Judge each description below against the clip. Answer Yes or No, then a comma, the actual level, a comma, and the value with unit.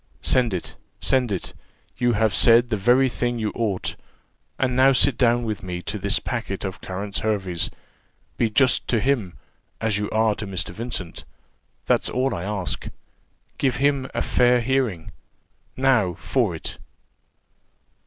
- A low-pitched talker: Yes, low, 110 Hz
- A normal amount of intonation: Yes, average, 4.2 semitones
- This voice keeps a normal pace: Yes, average, 155 wpm